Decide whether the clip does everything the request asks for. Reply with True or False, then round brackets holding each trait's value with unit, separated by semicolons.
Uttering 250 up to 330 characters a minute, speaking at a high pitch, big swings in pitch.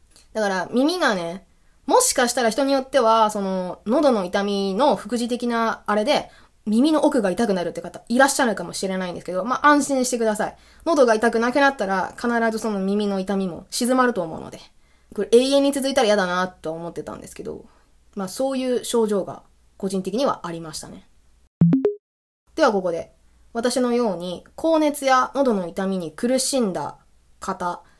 False (345 characters per minute; 225 Hz; 5.7 semitones)